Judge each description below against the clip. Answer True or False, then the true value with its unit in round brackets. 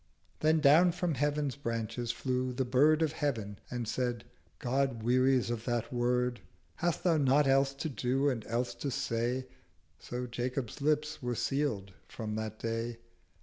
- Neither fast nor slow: True (155 wpm)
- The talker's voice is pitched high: False (125 Hz)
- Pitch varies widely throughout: False (3.3 semitones)